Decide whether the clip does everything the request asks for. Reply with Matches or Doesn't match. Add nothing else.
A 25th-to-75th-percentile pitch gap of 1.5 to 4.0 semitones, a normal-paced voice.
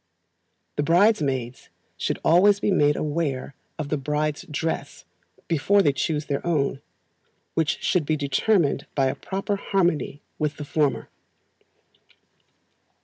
Doesn't match